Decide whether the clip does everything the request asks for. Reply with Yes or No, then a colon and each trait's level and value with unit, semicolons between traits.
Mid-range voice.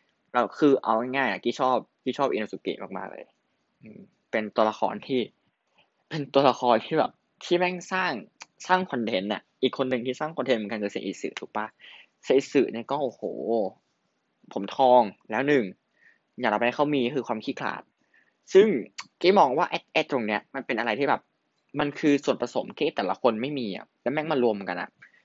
No: low, 130 Hz